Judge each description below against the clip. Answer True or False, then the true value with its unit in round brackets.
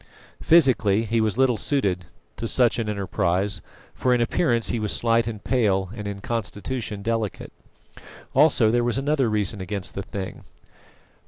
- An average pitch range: True (3.2 semitones)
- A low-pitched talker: True (110 Hz)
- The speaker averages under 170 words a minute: True (155 wpm)